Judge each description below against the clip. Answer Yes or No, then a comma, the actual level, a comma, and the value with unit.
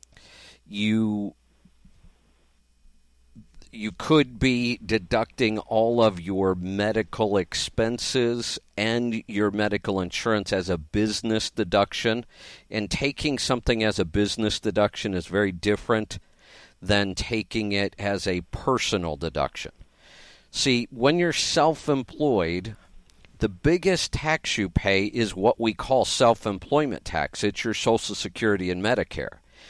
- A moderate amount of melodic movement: Yes, average, 3.4 semitones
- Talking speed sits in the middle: No, slow, 115 wpm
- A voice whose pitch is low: Yes, low, 105 Hz